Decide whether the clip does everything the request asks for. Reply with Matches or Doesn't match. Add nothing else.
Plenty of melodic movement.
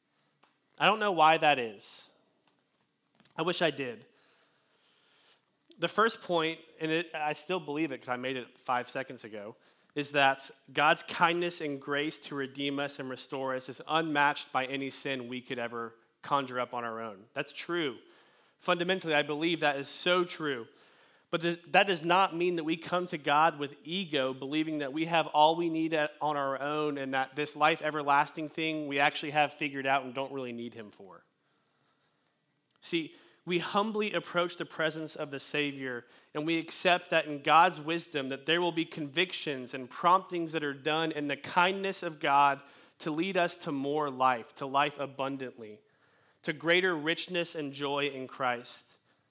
Doesn't match